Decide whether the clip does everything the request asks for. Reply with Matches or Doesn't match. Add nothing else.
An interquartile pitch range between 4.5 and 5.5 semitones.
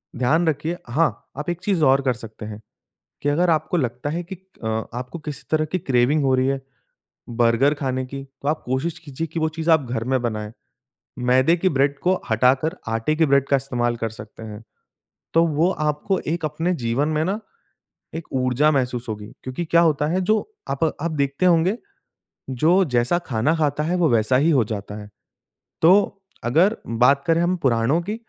Matches